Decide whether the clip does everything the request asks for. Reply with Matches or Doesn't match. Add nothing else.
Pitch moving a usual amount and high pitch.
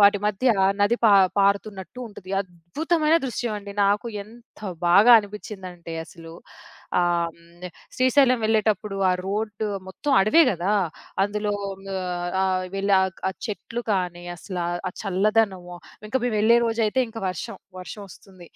Matches